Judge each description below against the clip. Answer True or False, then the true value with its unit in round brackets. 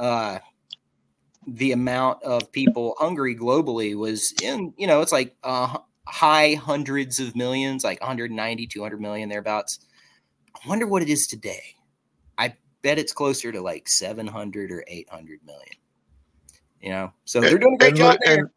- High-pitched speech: False (120 Hz)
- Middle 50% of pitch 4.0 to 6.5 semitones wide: True (4.6 semitones)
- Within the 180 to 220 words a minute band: False (155 wpm)